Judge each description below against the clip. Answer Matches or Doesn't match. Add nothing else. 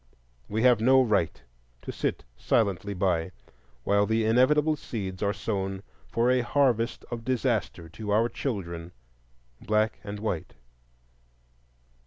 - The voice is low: Matches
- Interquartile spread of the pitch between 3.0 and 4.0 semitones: Matches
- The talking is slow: Matches